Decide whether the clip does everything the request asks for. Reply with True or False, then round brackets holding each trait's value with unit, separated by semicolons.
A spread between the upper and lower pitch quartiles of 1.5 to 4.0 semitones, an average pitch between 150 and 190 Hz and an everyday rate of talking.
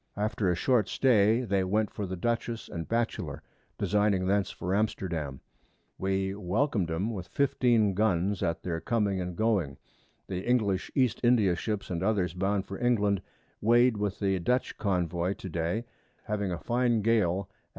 False (3.5 semitones; 100 Hz; 165 wpm)